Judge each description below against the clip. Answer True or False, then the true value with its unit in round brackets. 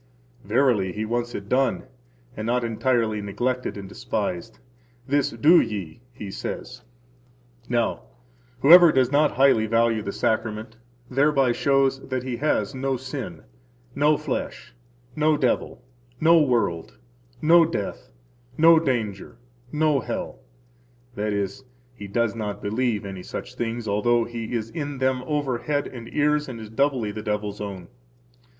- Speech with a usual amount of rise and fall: True (4.3 semitones)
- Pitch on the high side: False (120 Hz)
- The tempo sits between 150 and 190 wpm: False (140 wpm)